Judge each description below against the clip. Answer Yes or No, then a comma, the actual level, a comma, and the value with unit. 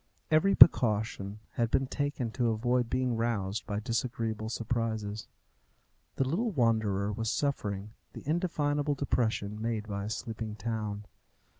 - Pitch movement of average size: Yes, average, 3.4 semitones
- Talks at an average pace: No, slow, 130 wpm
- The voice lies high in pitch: No, low, 115 Hz